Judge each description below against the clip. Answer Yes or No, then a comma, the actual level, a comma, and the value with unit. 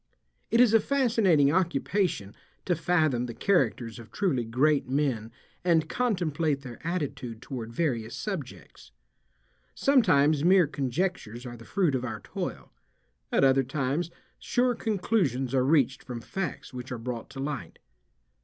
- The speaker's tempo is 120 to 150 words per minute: Yes, average, 140 wpm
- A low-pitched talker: No, medium, 145 Hz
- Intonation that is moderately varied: No, wide, 6.4 semitones